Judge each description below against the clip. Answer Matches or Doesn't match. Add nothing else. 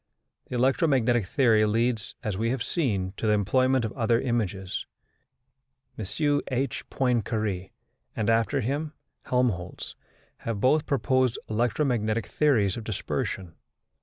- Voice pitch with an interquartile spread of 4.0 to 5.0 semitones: Doesn't match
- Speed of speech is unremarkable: Doesn't match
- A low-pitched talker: Matches